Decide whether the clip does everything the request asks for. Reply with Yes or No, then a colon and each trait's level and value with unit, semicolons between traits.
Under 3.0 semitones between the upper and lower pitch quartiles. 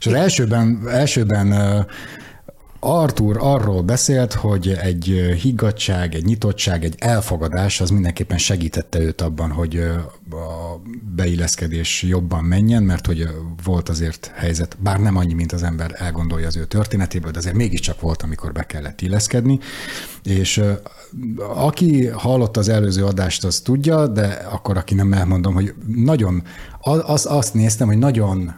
No: average, 4.8 semitones